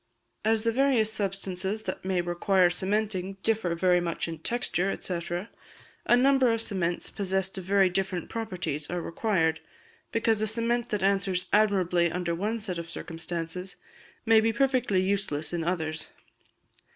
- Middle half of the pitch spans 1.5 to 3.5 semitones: No, average, 3.9 semitones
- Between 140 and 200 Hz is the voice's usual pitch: Yes, high, 190 Hz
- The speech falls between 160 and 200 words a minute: No, average, 150 wpm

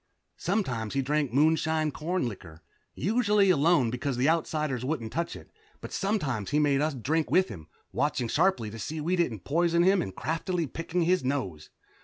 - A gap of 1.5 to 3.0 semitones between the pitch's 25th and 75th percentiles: No, average, 5.3 semitones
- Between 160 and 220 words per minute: Yes, average, 185 wpm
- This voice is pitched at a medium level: Yes, medium, 150 Hz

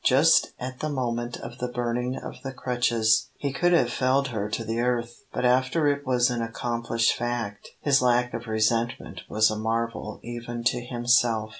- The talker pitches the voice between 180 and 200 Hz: No, low, 120 Hz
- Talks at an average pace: Yes, average, 180 wpm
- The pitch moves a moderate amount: No, narrow, 1.6 semitones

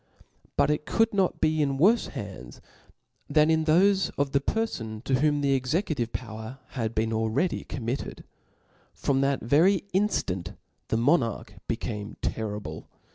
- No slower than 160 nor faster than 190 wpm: No, slow, 135 wpm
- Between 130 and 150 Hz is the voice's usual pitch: Yes, low, 135 Hz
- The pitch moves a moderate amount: No, wide, 6.0 semitones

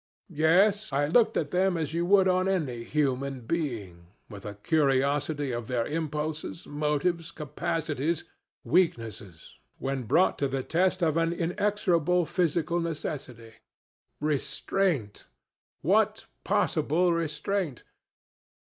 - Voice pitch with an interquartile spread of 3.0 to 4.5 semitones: Yes, average, 4.2 semitones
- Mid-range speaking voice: Yes, medium, 155 Hz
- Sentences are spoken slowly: Yes, slow, 115 wpm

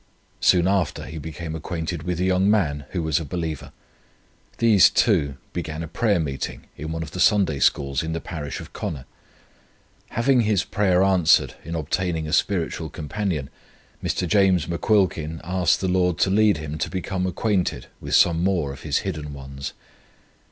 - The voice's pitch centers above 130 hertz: No, very low, 85 Hz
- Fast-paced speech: No, average, 170 wpm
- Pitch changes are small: No, average, 3.4 semitones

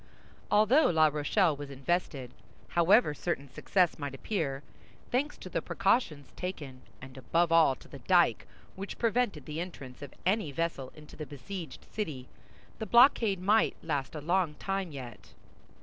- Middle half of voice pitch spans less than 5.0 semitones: No, wide, 5.6 semitones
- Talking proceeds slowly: No, average, 145 wpm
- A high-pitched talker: No, medium, 165 Hz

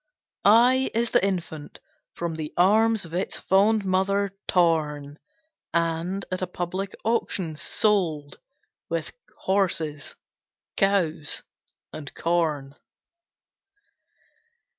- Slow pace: Yes, slow, 95 wpm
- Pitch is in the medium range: Yes, medium, 180 Hz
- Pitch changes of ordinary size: Yes, average, 3.8 semitones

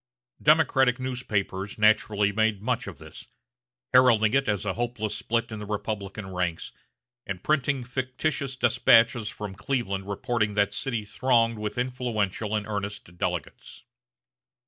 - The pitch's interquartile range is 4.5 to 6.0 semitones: No, average, 3.5 semitones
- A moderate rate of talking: No, slow, 130 wpm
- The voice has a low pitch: Yes, low, 110 Hz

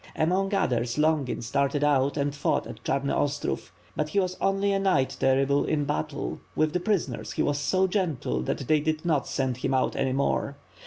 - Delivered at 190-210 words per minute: Yes, average, 195 wpm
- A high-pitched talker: No, medium, 145 Hz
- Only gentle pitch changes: No, average, 4.0 semitones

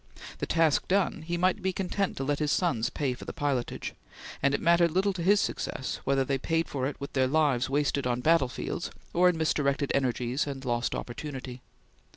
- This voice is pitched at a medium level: Yes, medium, 145 Hz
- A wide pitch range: No, average, 4.4 semitones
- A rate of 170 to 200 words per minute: Yes, average, 195 wpm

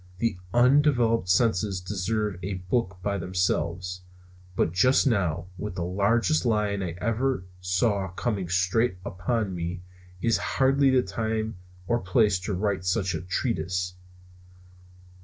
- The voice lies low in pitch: Yes, low, 100 Hz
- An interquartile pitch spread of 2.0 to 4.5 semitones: Yes, average, 4.1 semitones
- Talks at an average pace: No, slow, 130 wpm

